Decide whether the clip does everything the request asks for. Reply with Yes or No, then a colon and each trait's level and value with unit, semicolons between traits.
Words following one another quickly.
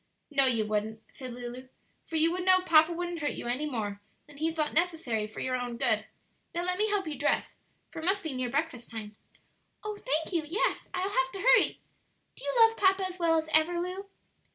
Yes: fast, 220 wpm